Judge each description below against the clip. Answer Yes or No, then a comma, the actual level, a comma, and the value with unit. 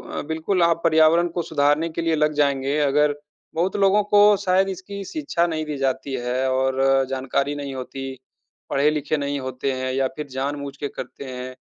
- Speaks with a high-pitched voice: No, medium, 145 Hz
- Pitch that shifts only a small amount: No, average, 3.8 semitones